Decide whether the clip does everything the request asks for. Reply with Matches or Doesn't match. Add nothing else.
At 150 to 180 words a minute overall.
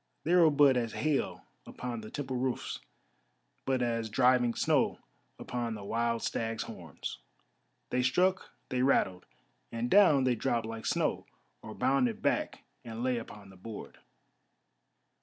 Doesn't match